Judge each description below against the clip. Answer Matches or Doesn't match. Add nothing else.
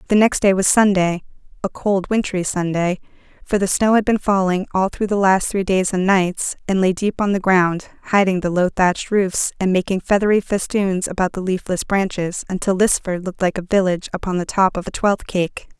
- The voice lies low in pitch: Doesn't match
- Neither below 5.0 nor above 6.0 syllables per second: Matches